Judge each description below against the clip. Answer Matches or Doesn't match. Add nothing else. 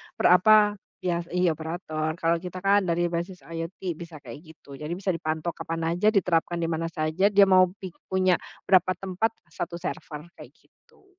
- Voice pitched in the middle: Matches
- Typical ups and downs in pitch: Doesn't match